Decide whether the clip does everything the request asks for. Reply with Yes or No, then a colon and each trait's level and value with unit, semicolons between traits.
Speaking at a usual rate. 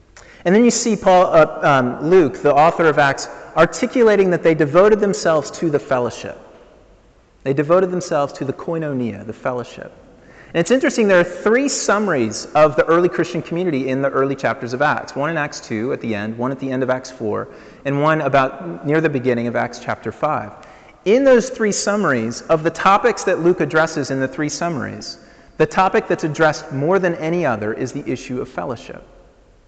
Yes: average, 195 wpm